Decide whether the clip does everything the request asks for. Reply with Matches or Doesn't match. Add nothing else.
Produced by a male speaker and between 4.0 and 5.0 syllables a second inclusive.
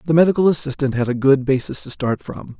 Doesn't match